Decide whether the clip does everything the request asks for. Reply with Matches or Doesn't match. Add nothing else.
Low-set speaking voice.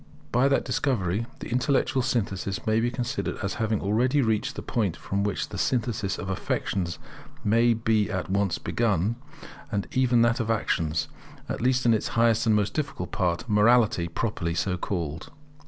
Matches